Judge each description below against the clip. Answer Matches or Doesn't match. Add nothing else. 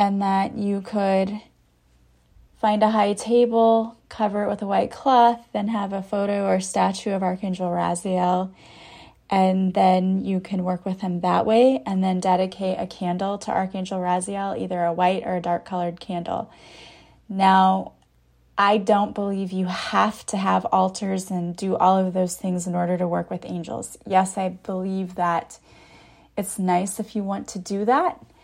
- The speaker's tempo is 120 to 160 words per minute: Doesn't match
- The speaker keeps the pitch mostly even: Matches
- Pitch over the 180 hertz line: Matches